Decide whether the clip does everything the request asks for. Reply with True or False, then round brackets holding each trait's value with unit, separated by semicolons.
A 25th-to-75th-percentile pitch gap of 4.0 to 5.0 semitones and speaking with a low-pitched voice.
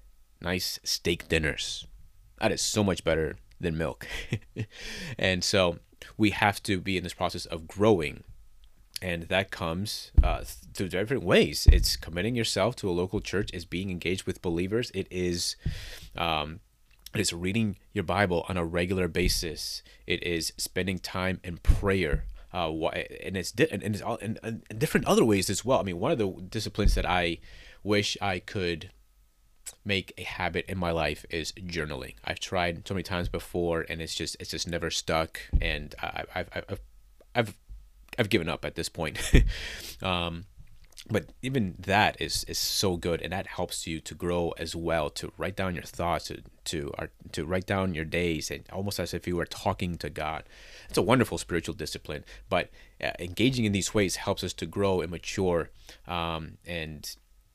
False (2.9 semitones; 90 Hz)